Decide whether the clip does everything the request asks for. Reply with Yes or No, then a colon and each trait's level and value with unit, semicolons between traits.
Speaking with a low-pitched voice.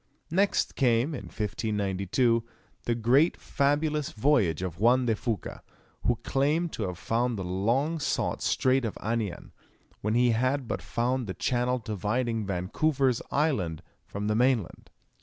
Yes: low, 120 Hz